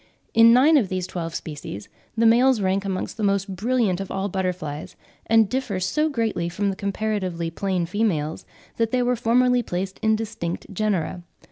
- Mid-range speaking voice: No, high, 200 Hz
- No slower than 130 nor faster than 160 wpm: No, average, 170 wpm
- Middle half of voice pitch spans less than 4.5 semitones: Yes, average, 3.9 semitones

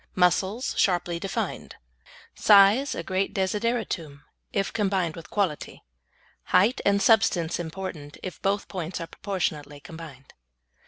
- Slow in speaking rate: Yes, slow, 115 wpm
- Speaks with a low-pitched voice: No, medium, 185 Hz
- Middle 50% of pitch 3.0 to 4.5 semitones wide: Yes, average, 3.4 semitones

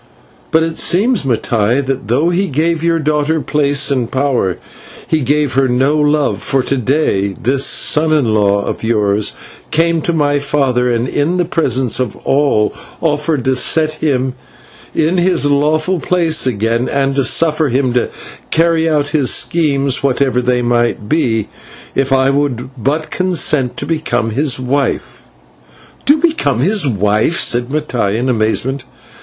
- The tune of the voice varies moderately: Yes, average, 4.1 semitones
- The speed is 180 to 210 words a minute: No, average, 160 wpm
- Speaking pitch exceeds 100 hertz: Yes, medium, 140 Hz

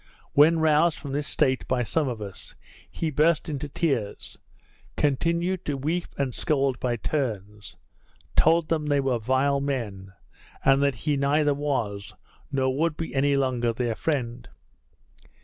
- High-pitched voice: No, medium, 140 Hz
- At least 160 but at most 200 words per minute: No, average, 150 wpm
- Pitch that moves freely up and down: No, average, 3.5 semitones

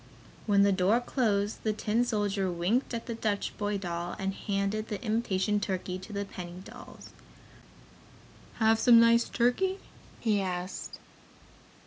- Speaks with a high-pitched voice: Yes, high, 205 Hz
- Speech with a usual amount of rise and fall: Yes, average, 3.0 semitones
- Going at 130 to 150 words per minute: Yes, average, 140 wpm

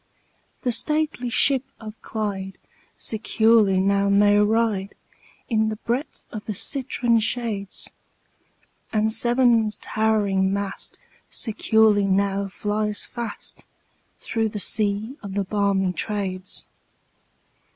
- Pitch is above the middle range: Yes, high, 215 Hz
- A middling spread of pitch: No, narrow, 2.2 semitones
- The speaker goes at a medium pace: No, slow, 105 wpm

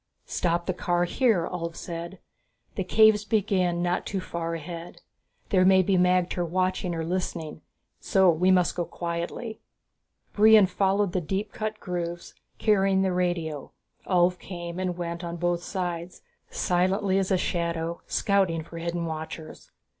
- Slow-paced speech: No, average, 145 wpm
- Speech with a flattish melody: Yes, narrow, 2.0 semitones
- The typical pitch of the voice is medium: Yes, medium, 180 Hz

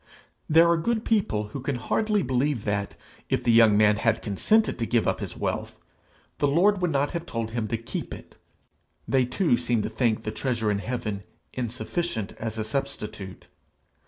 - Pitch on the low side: Yes, low, 120 Hz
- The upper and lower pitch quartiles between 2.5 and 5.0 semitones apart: No, wide, 5.5 semitones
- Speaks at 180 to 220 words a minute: Yes, average, 190 wpm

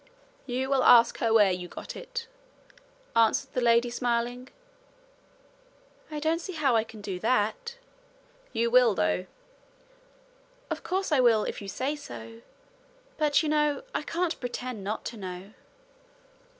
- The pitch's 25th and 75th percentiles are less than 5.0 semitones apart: No, average, 5.3 semitones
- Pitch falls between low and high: No, high, 245 Hz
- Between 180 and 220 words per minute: No, average, 145 wpm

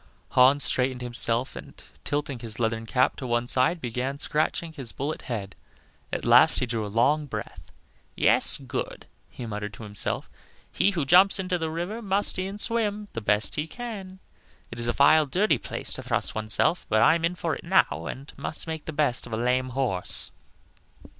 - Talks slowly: No, average, 190 wpm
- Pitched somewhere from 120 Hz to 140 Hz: Yes, low, 135 Hz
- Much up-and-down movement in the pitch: Yes, wide, 6.1 semitones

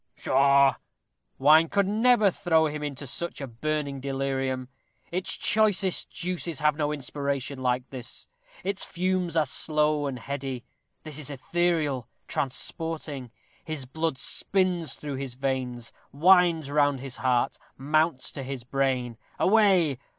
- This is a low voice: No, medium, 145 Hz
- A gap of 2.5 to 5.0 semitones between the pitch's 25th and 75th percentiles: Yes, average, 3.7 semitones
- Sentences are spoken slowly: Yes, slow, 130 wpm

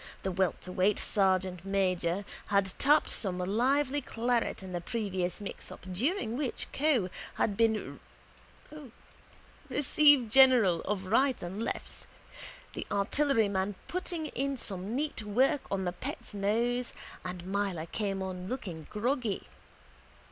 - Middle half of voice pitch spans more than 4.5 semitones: Yes, average, 5.1 semitones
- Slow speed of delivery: Yes, slow, 115 wpm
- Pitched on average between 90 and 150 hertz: No, high, 205 Hz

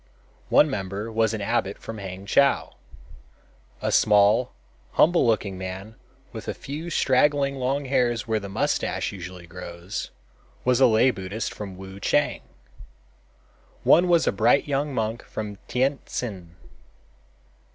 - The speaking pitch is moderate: No, low, 110 Hz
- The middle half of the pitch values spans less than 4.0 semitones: No, average, 5.3 semitones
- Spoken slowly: Yes, slow, 125 wpm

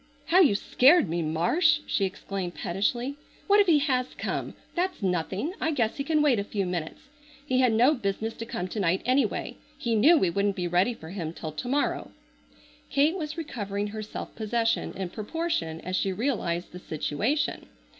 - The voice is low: No, high, 220 Hz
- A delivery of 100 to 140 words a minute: No, average, 185 wpm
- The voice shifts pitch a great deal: Yes, wide, 7.6 semitones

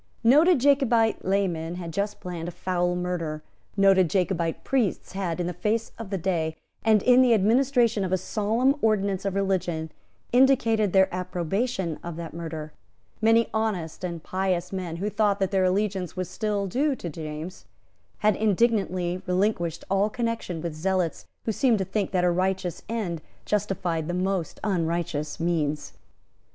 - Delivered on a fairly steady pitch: No, average, 3.7 semitones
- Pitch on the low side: No, high, 190 Hz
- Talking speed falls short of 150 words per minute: No, average, 155 wpm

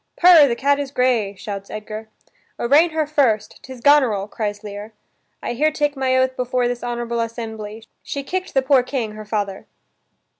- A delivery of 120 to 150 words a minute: No, average, 175 wpm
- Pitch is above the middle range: Yes, high, 245 Hz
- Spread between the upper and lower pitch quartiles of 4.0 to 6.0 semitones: Yes, average, 4.5 semitones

